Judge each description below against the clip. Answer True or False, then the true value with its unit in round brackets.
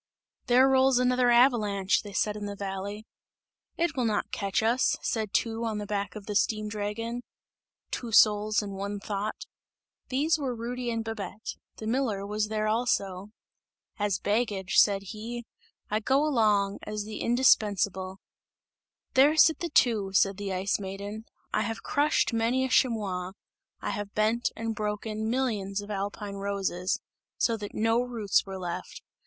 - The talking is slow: False (160 wpm)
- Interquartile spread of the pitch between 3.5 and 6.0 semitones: False (2.9 semitones)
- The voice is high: True (215 Hz)